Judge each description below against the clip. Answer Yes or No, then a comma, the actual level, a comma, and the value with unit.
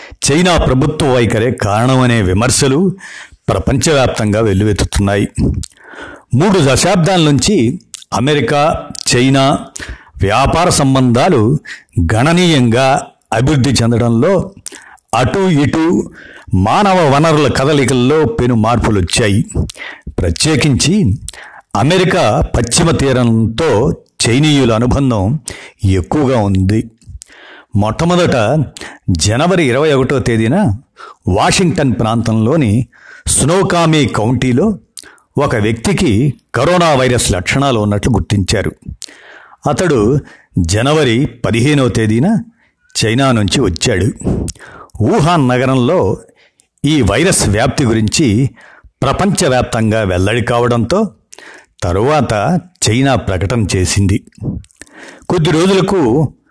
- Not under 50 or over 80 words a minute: Yes, average, 75 wpm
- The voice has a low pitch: Yes, low, 125 Hz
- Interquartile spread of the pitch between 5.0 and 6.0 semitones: Yes, average, 5.3 semitones